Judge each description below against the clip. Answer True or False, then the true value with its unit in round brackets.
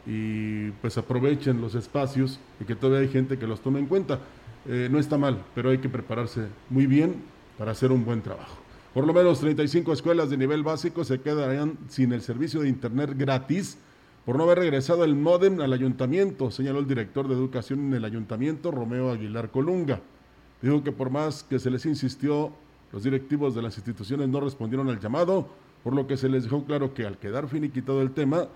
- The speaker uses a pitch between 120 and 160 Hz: True (135 Hz)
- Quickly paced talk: True (200 wpm)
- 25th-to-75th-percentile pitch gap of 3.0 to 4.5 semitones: True (3.3 semitones)